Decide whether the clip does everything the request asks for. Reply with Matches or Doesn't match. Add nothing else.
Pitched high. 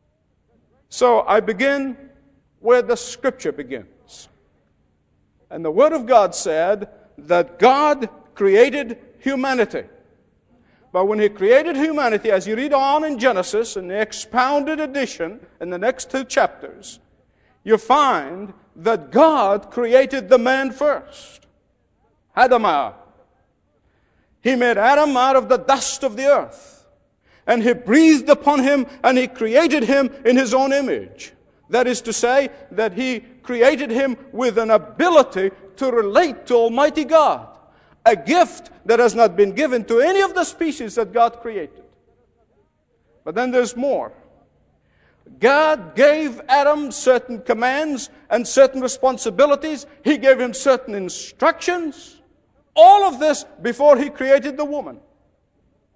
Matches